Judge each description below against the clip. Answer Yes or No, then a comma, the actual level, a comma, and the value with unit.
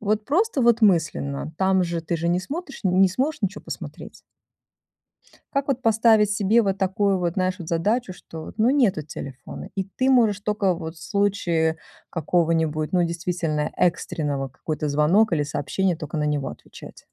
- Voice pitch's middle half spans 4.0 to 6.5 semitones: Yes, average, 4.7 semitones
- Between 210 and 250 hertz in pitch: No, medium, 185 Hz